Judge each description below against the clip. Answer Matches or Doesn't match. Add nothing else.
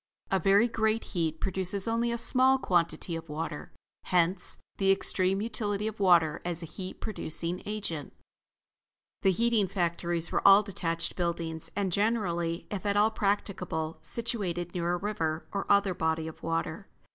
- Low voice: Doesn't match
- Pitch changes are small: Doesn't match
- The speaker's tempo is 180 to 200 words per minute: Doesn't match